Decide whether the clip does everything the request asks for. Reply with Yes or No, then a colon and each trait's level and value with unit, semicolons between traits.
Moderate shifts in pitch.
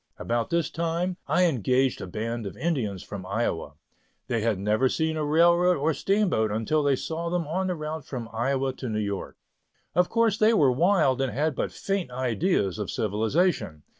No: wide, 7.2 semitones